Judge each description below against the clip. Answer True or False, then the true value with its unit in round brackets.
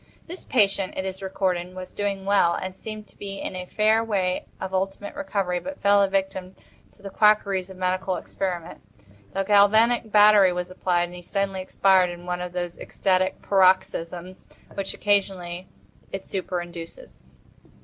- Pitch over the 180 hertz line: True (190 Hz)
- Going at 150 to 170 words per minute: True (160 wpm)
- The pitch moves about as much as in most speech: False (1.8 semitones)